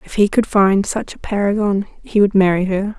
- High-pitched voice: Yes, high, 200 Hz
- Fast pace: Yes, fast, 220 wpm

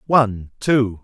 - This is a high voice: No, low, 115 Hz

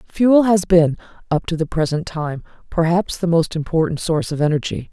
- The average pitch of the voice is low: No, medium, 165 Hz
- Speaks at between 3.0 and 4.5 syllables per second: No, 5.5 syllables/s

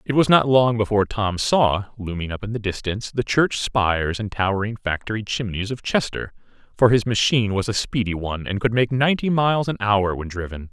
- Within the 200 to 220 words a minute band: Yes, fast, 205 wpm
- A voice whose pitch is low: Yes, low, 110 Hz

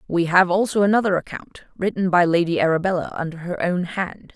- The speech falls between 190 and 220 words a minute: No, average, 180 wpm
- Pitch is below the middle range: No, medium, 180 Hz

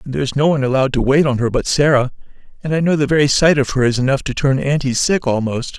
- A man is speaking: Yes, male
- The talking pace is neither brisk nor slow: No, fast, 280 wpm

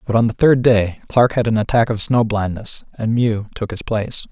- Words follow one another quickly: Yes, fast, 235 wpm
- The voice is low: Yes, low, 110 Hz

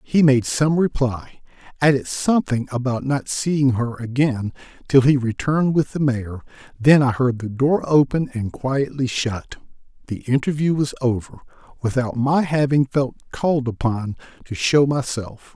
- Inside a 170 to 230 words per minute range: No, average, 150 wpm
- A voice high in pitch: No, low, 130 Hz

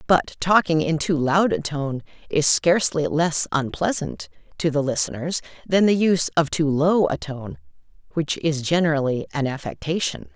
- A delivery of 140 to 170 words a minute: Yes, average, 155 wpm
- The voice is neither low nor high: Yes, medium, 155 Hz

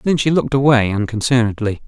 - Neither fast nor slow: Yes, average, 160 wpm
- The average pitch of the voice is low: Yes, low, 120 Hz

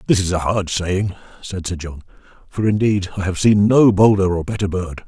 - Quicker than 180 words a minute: Yes, average, 200 wpm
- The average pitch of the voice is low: Yes, very low, 95 Hz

